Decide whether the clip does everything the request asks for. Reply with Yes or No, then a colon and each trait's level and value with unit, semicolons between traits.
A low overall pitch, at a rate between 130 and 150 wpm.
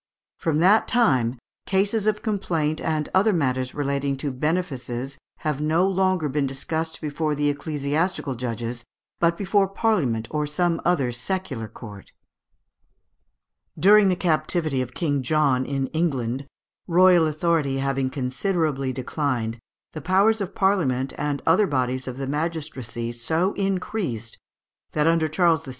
No: medium, 150 Hz; slow, 135 wpm